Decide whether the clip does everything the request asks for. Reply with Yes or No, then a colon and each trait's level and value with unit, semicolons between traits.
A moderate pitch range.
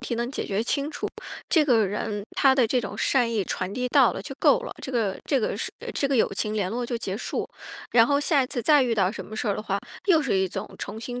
Yes: average, 4.2 semitones